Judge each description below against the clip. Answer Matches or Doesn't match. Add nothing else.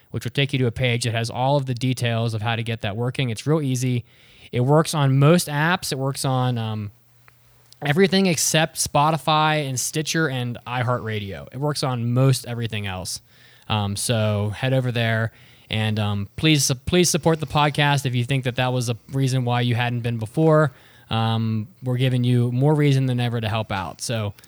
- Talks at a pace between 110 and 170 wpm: Doesn't match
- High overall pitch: Doesn't match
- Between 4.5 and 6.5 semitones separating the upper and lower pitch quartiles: Doesn't match